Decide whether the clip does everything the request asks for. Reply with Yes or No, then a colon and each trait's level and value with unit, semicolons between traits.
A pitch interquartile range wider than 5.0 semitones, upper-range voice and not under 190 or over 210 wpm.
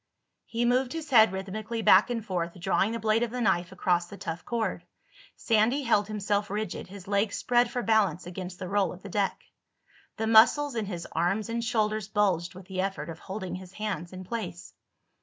No: average, 3.4 semitones; high, 205 Hz; average, 195 wpm